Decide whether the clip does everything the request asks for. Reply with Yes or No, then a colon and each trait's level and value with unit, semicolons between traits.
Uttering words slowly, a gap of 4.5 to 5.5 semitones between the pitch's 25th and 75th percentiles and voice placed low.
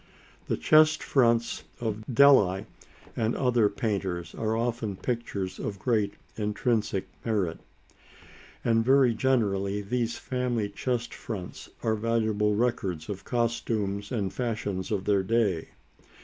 No: slow, 120 wpm; average, 2.9 semitones; low, 110 Hz